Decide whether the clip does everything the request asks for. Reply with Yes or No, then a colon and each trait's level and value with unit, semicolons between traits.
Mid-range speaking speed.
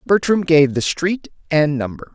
Yes: average, 170 wpm